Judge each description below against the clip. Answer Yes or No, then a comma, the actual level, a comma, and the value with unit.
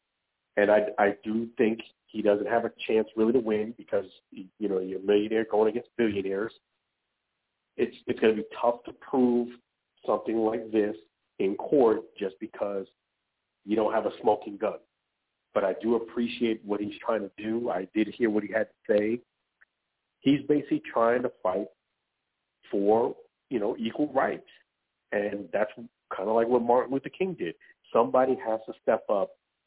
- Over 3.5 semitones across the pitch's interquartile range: No, narrow, 2.5 semitones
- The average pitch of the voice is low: Yes, low, 110 Hz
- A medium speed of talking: Yes, average, 170 wpm